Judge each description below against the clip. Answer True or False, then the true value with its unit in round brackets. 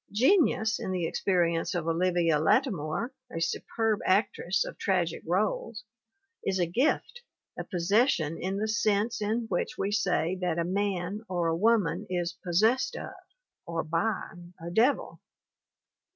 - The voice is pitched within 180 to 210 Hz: True (190 Hz)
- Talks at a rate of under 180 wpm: True (140 wpm)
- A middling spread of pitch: True (4.3 semitones)